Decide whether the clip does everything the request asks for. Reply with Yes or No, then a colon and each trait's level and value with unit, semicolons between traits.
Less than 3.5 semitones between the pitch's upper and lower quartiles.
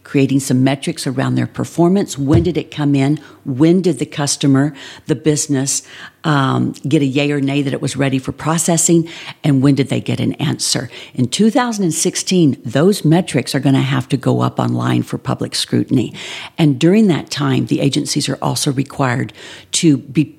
Yes: average, 2.9 semitones